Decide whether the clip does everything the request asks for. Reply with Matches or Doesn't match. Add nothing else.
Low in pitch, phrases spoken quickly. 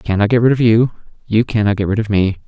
Matches